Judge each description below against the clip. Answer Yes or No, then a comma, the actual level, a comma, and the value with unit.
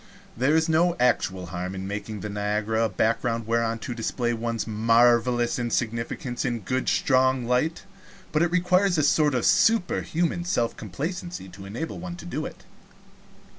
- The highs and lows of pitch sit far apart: Yes, wide, 5.9 semitones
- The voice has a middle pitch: No, low, 120 Hz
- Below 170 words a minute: Yes, average, 160 wpm